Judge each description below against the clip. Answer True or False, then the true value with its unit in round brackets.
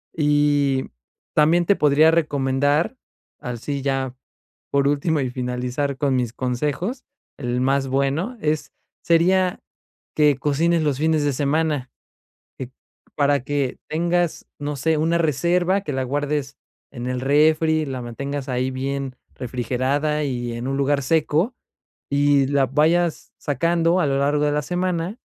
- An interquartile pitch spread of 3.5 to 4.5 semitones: False (3.1 semitones)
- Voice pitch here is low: False (145 Hz)